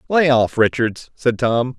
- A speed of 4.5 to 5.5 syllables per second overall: No, 3.9 syllables/s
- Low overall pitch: Yes, low, 125 Hz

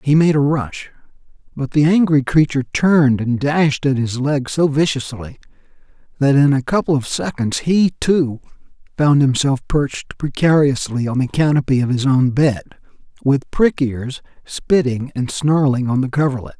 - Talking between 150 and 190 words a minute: Yes, average, 160 wpm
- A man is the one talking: Yes, male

